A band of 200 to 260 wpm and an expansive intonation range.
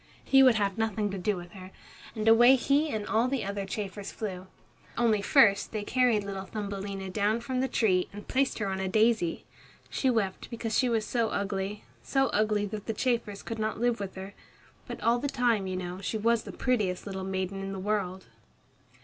No: fast, 205 wpm; average, 3.2 semitones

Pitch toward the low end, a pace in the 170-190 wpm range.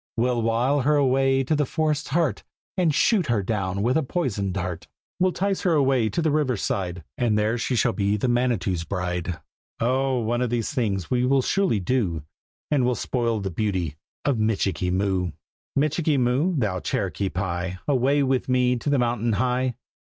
Yes: low, 120 Hz; average, 185 wpm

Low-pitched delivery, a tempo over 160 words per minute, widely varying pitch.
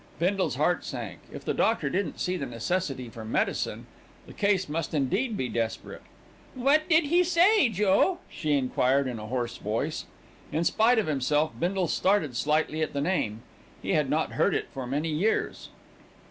No: medium, 160 Hz; average, 175 wpm; wide, 7.5 semitones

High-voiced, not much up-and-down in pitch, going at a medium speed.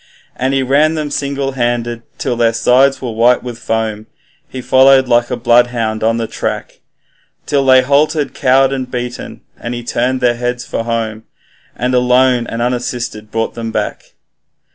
No: low, 125 Hz; narrow, 2.0 semitones; average, 165 wpm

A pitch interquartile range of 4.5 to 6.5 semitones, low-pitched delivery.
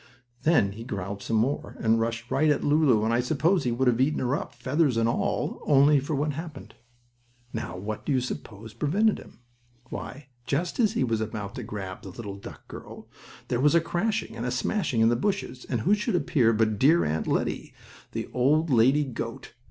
Yes: average, 5.1 semitones; low, 125 Hz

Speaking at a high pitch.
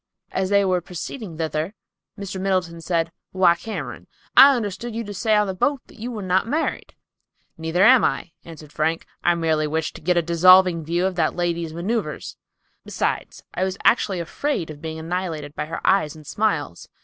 No: medium, 175 Hz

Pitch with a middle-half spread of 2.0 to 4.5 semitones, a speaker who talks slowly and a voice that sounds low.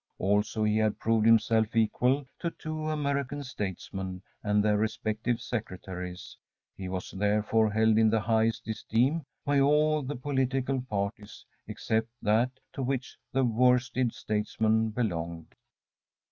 Yes: average, 3.6 semitones; slow, 130 wpm; low, 110 Hz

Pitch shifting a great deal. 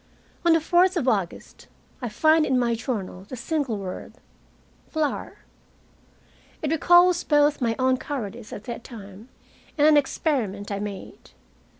Yes: wide, 6.7 semitones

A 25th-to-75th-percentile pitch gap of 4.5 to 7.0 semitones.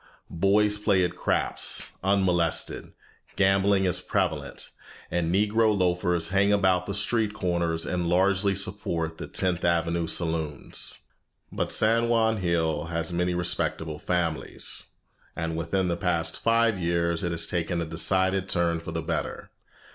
No: average, 2.8 semitones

